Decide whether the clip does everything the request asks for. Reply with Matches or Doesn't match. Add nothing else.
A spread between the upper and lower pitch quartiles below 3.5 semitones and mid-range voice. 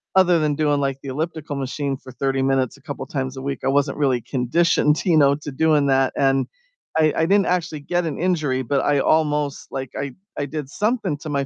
Matches